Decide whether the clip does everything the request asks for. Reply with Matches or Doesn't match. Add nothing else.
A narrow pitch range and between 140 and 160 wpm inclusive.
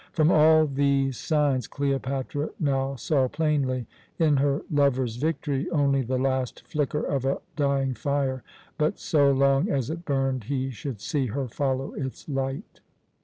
Matches